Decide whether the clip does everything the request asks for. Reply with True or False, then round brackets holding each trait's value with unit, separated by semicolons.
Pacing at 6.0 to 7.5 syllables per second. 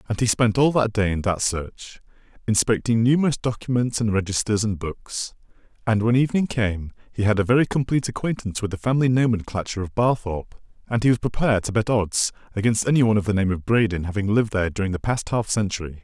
True (6.5 syllables/s)